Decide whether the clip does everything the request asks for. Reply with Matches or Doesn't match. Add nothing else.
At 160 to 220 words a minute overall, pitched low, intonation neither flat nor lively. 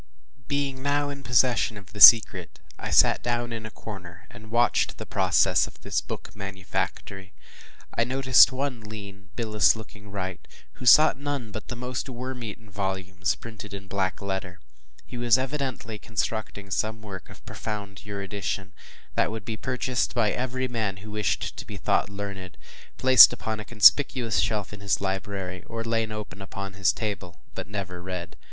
Matches